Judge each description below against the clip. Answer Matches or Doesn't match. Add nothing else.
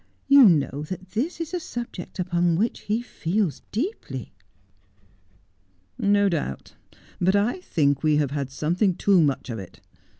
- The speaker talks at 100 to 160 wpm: Matches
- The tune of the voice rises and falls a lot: Matches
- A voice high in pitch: Doesn't match